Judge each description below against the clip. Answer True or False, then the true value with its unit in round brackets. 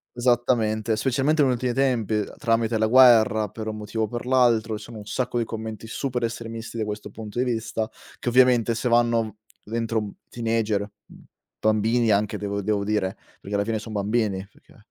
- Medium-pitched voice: False (115 Hz)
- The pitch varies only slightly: True (2.0 semitones)